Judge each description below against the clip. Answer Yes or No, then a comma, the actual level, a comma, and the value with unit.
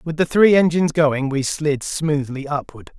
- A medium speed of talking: Yes, average, 180 wpm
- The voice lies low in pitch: No, medium, 150 Hz